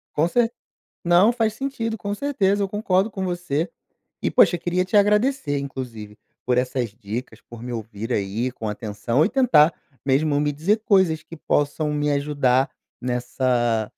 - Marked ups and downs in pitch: Yes, wide, 8.0 semitones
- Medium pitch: Yes, medium, 150 Hz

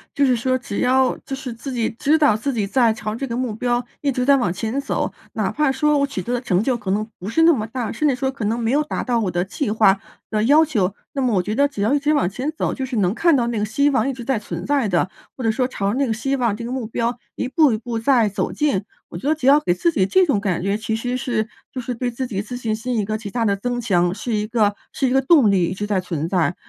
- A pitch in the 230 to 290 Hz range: Yes, high, 240 Hz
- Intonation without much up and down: No, average, 4.1 semitones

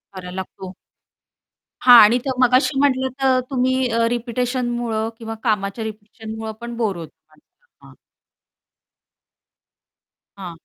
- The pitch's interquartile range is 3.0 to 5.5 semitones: No, narrow, 2.6 semitones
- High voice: Yes, high, 235 Hz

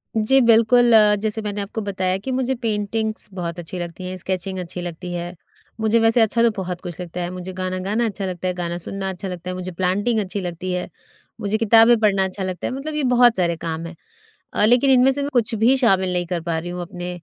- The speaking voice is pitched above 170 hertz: Yes, high, 190 Hz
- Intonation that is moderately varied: Yes, average, 4.0 semitones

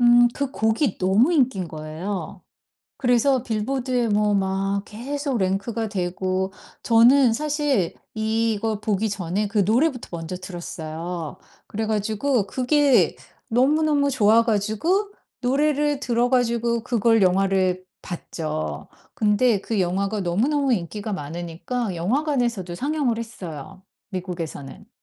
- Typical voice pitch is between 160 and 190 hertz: No, high, 220 Hz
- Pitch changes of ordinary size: Yes, average, 4.9 semitones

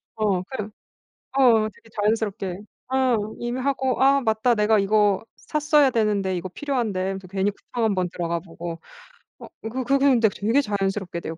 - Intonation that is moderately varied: Yes, average, 4.8 semitones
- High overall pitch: Yes, high, 215 Hz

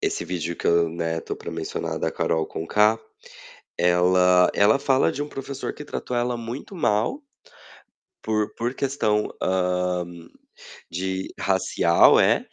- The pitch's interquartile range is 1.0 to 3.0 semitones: No, average, 5.3 semitones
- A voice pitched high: No, very low, 95 Hz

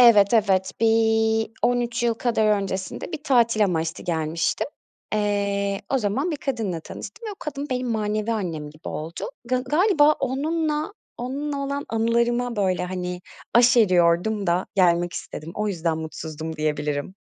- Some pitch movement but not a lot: No, wide, 5.8 semitones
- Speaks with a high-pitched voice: Yes, high, 210 Hz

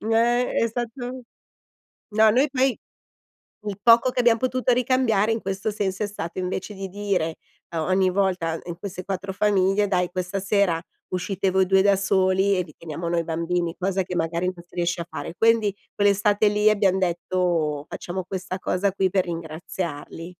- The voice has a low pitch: No, high, 190 Hz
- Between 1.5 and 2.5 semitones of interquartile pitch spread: No, average, 2.9 semitones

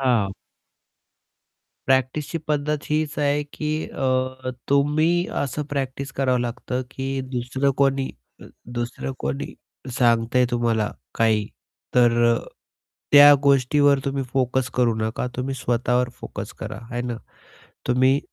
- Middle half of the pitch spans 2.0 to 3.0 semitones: Yes, narrow, 2.5 semitones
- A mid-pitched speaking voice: No, low, 130 Hz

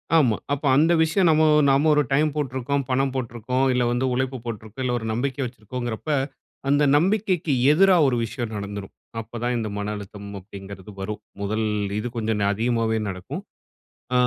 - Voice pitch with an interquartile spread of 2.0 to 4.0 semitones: No, average, 4.5 semitones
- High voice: No, low, 120 Hz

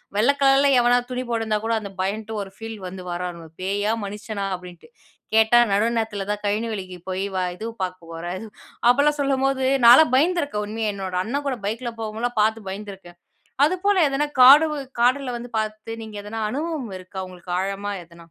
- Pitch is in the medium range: No, high, 220 Hz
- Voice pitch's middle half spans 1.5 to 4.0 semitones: No, average, 4.5 semitones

